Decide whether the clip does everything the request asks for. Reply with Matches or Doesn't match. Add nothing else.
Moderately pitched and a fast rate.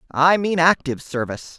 Doesn't match